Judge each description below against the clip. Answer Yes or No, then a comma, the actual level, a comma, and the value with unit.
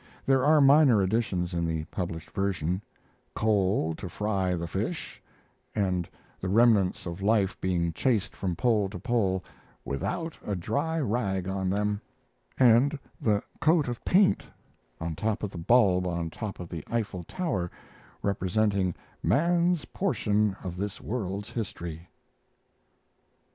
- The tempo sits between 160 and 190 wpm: No, slow, 135 wpm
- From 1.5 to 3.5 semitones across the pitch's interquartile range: No, average, 4.5 semitones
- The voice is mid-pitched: No, low, 100 Hz